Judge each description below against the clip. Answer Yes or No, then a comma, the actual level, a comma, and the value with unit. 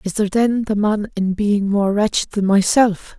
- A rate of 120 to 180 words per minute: No, fast, 205 wpm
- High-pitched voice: Yes, high, 205 Hz